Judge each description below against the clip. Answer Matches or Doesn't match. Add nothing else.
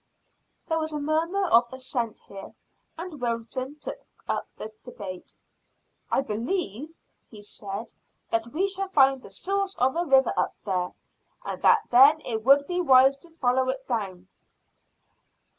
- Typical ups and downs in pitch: Doesn't match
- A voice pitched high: Matches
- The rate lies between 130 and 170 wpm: Matches